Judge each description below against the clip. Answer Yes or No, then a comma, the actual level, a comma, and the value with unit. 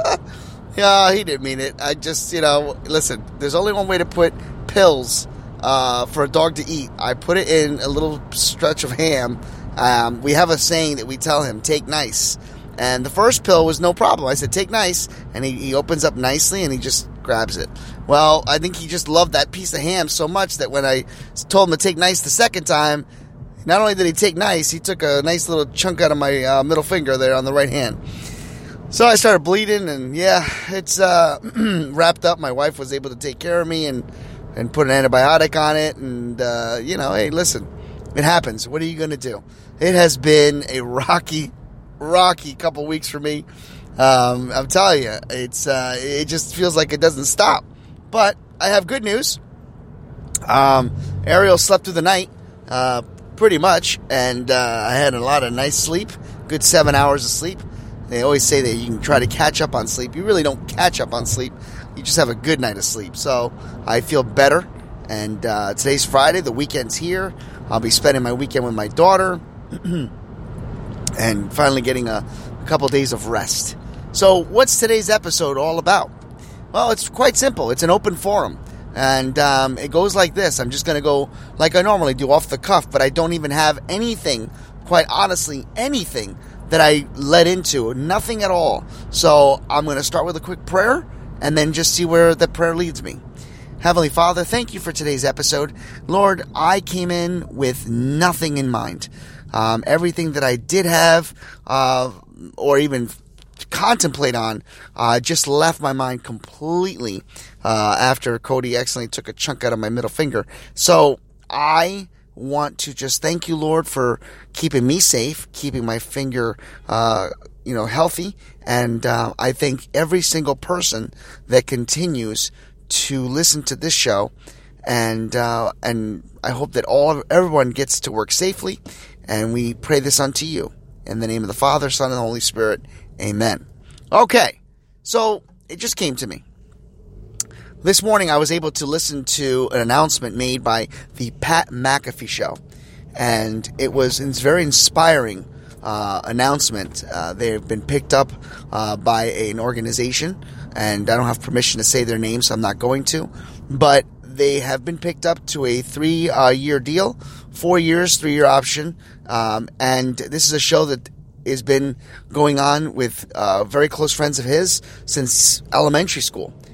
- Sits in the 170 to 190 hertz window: No, medium, 140 Hz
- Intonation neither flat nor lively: Yes, average, 4.9 semitones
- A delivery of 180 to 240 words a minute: Yes, average, 190 wpm